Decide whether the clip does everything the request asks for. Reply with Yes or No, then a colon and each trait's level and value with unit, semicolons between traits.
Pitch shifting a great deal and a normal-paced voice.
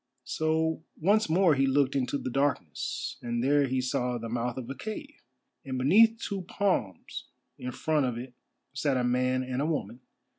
No: average, 4.1 semitones; average, 180 wpm